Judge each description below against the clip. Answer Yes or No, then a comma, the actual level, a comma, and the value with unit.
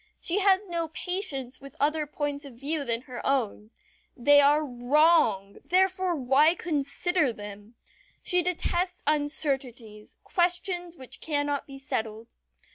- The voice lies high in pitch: Yes, very high, 290 Hz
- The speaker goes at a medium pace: No, slow, 125 wpm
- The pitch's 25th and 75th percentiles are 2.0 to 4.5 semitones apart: No, wide, 5.5 semitones